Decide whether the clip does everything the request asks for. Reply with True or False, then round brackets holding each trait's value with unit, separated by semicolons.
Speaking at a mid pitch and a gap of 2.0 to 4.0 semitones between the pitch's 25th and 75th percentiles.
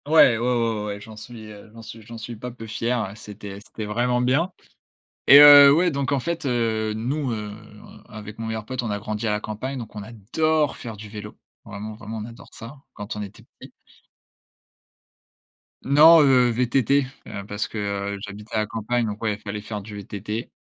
False (110 Hz; 2.9 semitones)